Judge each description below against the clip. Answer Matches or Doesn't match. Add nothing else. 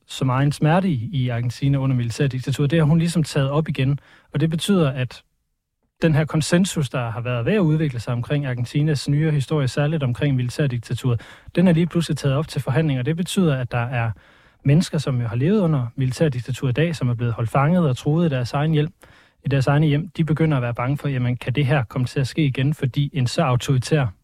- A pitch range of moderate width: Matches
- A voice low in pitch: Doesn't match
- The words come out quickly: Matches